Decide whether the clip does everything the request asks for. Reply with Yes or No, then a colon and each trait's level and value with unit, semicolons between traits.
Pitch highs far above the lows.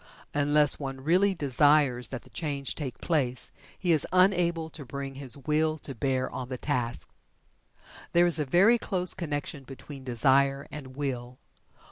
No: average, 3.2 semitones